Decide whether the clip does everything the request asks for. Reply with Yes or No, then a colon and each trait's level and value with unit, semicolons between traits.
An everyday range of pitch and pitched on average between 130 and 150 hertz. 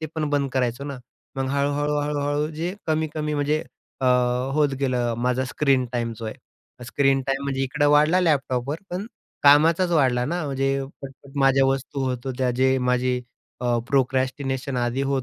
No: narrow, 2.3 semitones; low, 135 Hz